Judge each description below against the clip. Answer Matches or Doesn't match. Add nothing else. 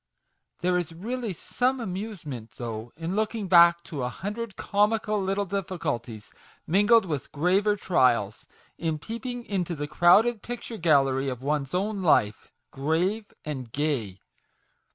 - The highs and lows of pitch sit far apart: Matches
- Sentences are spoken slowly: Matches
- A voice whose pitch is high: Doesn't match